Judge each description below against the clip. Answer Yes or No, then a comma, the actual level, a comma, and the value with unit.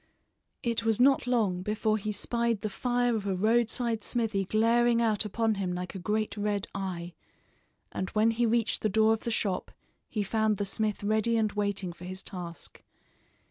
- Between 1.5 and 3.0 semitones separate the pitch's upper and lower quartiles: Yes, narrow, 2.6 semitones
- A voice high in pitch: Yes, high, 215 Hz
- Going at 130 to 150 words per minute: No, average, 180 wpm